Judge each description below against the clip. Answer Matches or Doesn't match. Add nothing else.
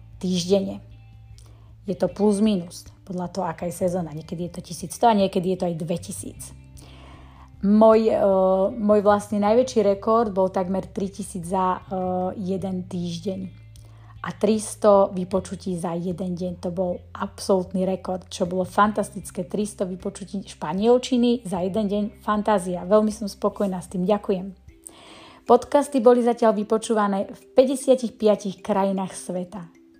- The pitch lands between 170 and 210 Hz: Matches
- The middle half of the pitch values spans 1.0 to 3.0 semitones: Matches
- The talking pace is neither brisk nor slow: Matches